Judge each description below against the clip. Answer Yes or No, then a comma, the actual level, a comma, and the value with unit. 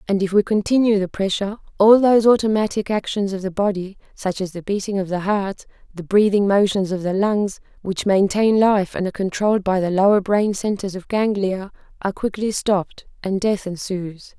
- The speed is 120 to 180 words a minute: No, average, 190 wpm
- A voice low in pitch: No, high, 200 Hz